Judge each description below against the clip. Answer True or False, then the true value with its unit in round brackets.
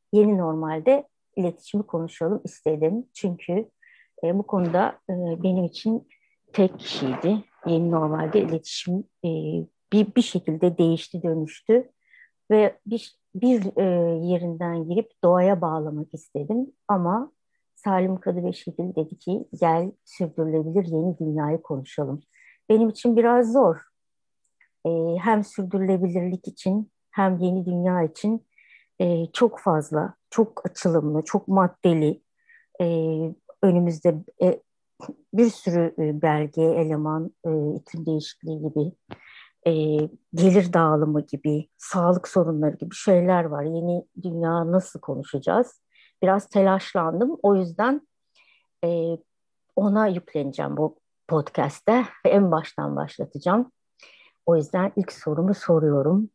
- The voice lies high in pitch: False (180 Hz)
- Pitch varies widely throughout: False (4.1 semitones)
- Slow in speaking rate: False (105 wpm)